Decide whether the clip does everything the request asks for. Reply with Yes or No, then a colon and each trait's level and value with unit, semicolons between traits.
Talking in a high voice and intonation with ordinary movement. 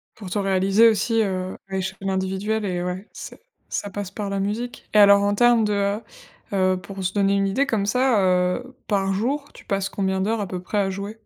No: high, 200 Hz; narrow, 1.9 semitones